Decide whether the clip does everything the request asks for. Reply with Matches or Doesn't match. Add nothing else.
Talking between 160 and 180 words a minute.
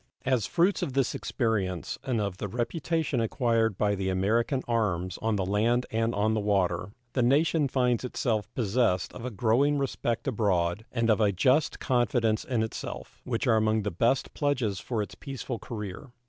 Matches